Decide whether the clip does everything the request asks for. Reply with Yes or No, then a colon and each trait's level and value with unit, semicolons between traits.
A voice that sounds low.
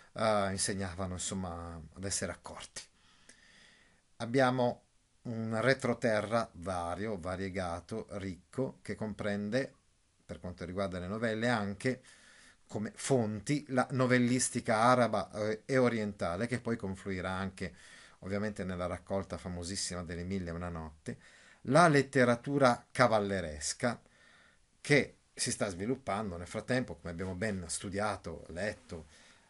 Yes: low, 100 Hz